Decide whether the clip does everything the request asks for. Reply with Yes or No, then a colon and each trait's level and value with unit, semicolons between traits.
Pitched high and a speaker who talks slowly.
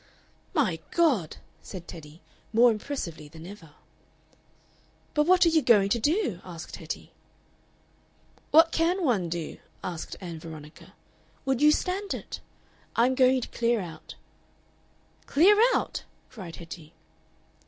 Yes: high, 225 Hz; slow, 125 wpm